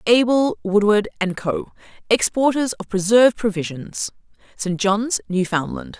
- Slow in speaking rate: Yes, slow, 110 wpm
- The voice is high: Yes, high, 215 Hz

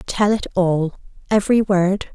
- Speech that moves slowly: Yes, slow, 110 wpm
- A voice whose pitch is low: No, high, 190 Hz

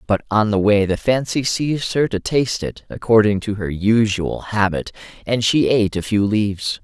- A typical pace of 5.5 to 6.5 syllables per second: No, 5.0 syllables/s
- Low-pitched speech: Yes, low, 110 Hz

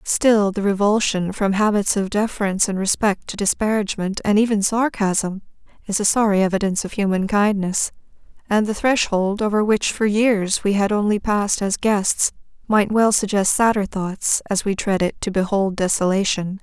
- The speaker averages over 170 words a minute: No, average, 165 wpm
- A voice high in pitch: Yes, high, 205 Hz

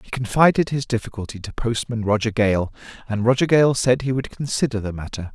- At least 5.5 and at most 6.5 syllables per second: Yes, 5.7 syllables/s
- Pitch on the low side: Yes, low, 115 Hz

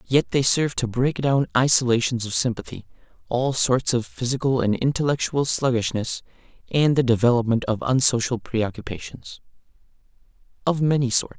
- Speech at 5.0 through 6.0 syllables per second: Yes, 5.2 syllables/s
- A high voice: No, low, 125 Hz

